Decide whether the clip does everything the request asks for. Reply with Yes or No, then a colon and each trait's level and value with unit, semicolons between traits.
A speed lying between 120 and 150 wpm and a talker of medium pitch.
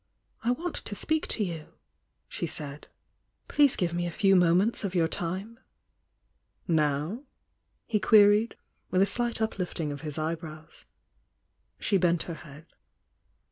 Yes: average, 140 wpm; medium, 180 Hz